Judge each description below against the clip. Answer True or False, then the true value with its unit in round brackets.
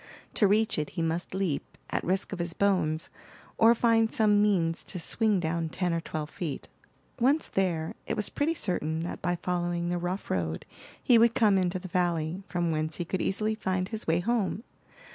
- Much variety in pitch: False (4.0 semitones)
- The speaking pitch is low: False (180 Hz)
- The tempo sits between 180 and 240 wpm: True (195 wpm)